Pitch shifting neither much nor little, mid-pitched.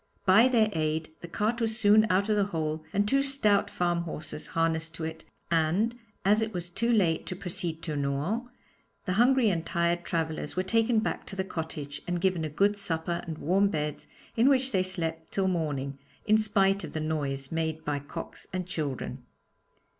Yes: average, 4.5 semitones; medium, 175 Hz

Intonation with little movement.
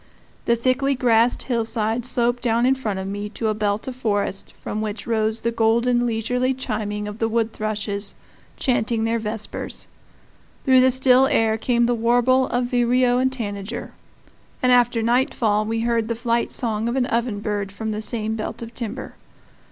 Yes: narrow, 2.3 semitones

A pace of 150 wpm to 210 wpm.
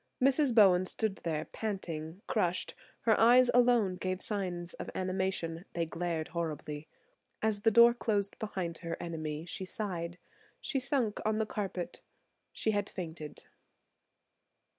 No: slow, 135 wpm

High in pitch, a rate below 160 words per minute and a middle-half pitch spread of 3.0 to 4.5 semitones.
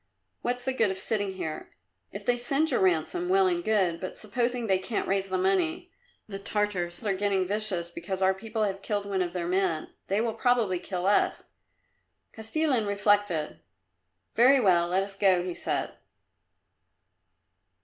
No: high, 200 Hz; average, 165 wpm; average, 3.3 semitones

